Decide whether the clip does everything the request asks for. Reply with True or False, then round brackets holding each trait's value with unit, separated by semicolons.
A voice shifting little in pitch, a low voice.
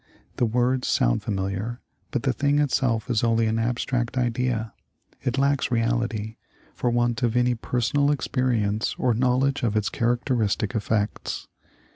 True (2.3 semitones; 120 Hz)